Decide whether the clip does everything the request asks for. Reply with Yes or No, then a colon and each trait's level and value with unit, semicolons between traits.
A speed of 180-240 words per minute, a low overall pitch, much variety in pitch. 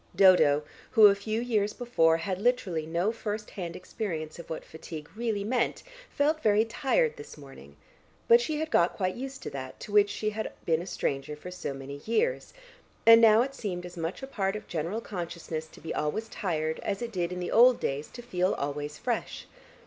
No: average, 200 wpm; high, 190 Hz; wide, 6.0 semitones